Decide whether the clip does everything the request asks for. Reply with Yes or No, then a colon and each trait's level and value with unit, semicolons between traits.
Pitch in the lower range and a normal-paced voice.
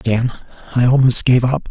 Yes: low, 125 Hz; average, 175 wpm